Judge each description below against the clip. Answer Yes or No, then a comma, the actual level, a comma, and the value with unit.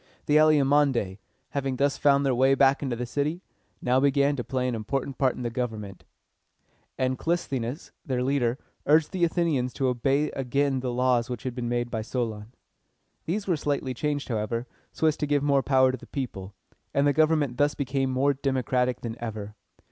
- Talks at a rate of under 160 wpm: No, average, 190 wpm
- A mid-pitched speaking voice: No, low, 130 Hz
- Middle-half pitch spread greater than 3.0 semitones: No, average, 2.7 semitones